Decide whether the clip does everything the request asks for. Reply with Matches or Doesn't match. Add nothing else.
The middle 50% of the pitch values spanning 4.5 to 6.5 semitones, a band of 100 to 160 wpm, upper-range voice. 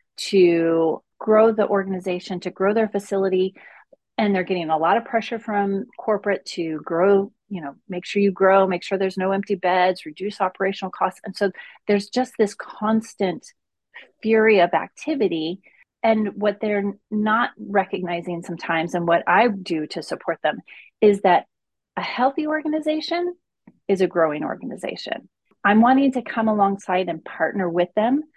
Doesn't match